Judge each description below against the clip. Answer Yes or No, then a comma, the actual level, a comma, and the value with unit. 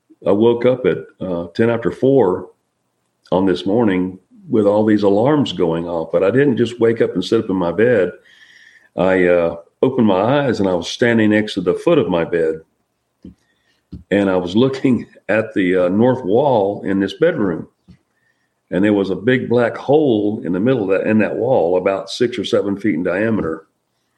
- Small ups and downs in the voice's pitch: No, average, 4.2 semitones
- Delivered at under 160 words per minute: No, average, 195 wpm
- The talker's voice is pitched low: Yes, low, 100 Hz